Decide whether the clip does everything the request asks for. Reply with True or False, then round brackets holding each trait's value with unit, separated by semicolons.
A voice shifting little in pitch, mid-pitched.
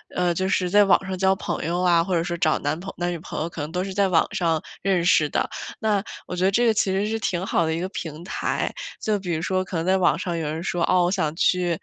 True (2.2 semitones; 180 Hz)